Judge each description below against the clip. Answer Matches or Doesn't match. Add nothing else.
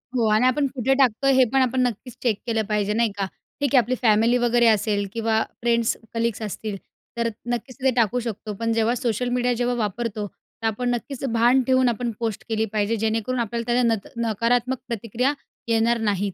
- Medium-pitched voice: Doesn't match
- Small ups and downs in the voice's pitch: Matches